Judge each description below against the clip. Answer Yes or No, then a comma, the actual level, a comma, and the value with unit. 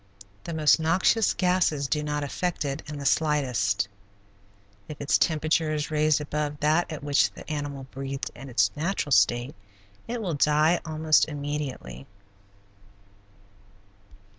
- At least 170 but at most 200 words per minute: No, slow, 135 wpm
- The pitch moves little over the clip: Yes, narrow, 2.2 semitones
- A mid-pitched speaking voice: Yes, medium, 150 Hz